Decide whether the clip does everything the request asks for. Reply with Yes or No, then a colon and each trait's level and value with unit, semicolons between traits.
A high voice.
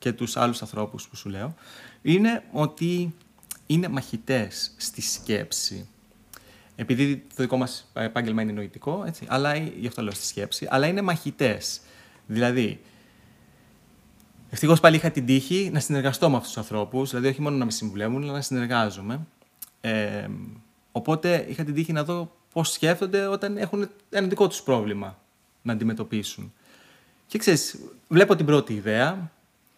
No: low, 135 Hz